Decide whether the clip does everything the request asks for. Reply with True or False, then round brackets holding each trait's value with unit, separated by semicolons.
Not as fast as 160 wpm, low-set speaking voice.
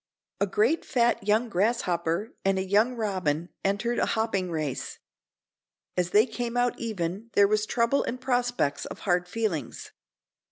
False (150 wpm; 210 Hz)